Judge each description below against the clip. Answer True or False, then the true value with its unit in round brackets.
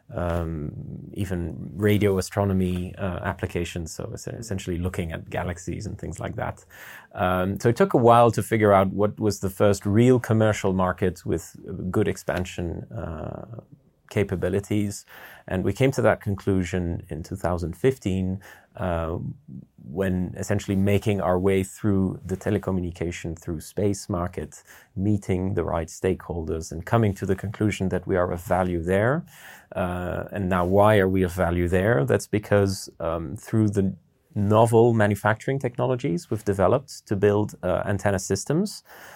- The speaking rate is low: False (145 wpm)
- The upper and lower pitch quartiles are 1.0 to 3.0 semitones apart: True (2.7 semitones)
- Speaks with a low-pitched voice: True (95 Hz)